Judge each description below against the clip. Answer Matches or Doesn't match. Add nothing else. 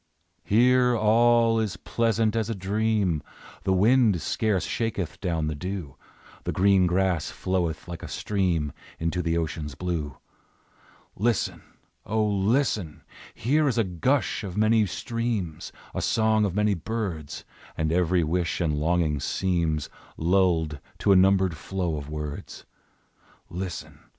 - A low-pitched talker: Matches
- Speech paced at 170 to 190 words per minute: Doesn't match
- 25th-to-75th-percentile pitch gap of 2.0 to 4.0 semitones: Doesn't match